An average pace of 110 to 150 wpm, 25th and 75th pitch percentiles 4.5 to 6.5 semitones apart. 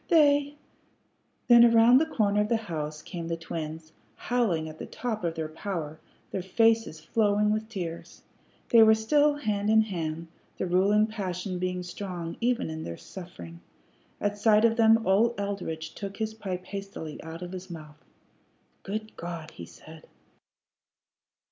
No: average, 160 wpm; average, 5.0 semitones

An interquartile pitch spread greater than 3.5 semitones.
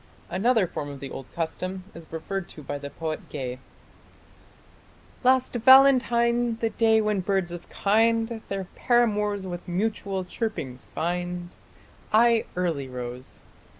Yes: wide, 5.6 semitones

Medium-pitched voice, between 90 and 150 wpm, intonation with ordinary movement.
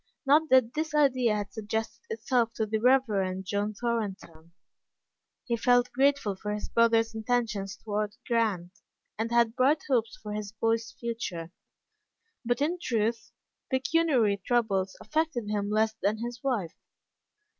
No: high, 225 Hz; average, 140 wpm; average, 3.2 semitones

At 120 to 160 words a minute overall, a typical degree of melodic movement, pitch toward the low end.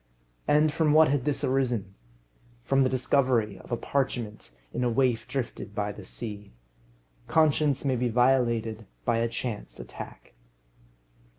Yes: average, 140 wpm; average, 3.4 semitones; low, 125 Hz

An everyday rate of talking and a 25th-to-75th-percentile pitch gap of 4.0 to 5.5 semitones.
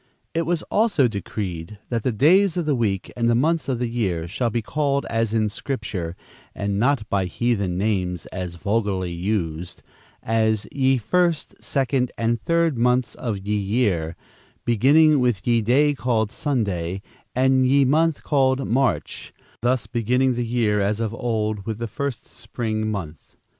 Yes: average, 165 wpm; average, 4.5 semitones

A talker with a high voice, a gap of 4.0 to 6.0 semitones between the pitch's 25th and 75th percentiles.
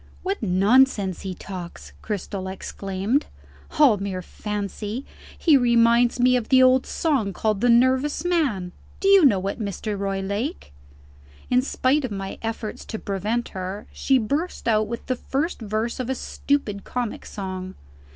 Yes: high, 220 Hz; average, 4.8 semitones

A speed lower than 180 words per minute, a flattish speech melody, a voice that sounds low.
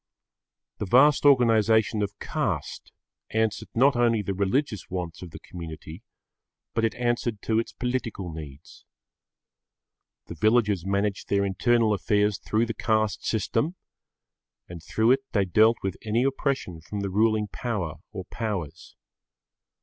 No: slow, 135 wpm; average, 3.3 semitones; low, 110 Hz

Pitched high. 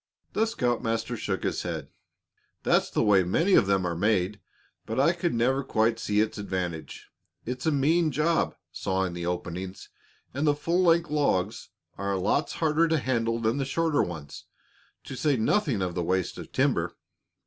No: low, 115 Hz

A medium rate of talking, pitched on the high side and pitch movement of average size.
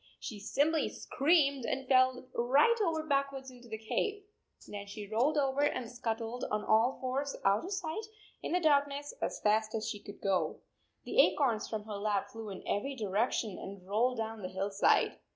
Yes: average, 180 wpm; high, 245 Hz; average, 4.9 semitones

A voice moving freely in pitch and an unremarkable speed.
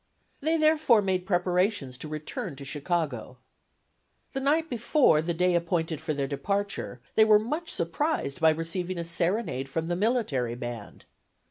Yes: wide, 6.2 semitones; average, 150 wpm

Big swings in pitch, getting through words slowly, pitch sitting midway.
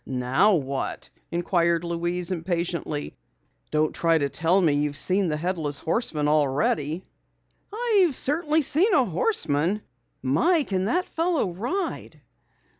Yes: wide, 8.3 semitones; slow, 120 wpm; medium, 175 Hz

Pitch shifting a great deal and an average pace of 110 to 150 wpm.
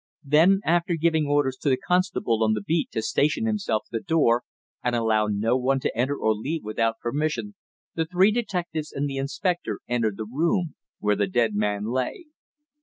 No: wide, 6.6 semitones; average, 185 wpm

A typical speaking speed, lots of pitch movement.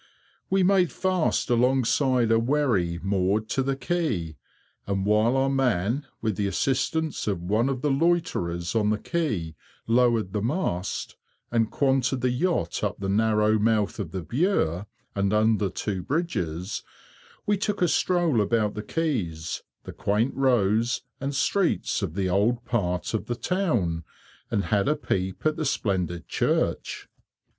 Yes: average, 150 wpm; wide, 5.8 semitones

